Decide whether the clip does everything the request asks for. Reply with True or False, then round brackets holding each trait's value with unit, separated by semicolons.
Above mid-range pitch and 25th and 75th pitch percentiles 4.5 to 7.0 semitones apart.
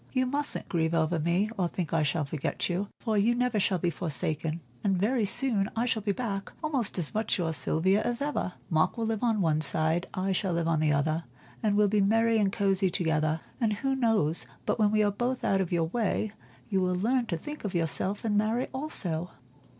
True (195 Hz; 5.2 semitones)